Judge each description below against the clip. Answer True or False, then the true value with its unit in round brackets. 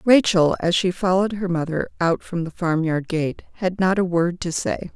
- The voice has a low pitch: False (175 Hz)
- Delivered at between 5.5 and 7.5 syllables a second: False (4.9 syllables/s)